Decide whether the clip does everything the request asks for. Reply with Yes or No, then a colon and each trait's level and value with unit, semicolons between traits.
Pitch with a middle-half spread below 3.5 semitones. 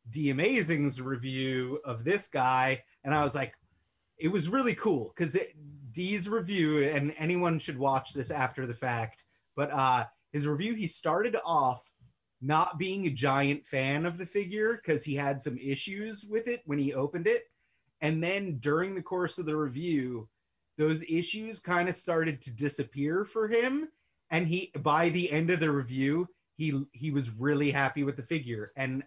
No: average, 4.6 semitones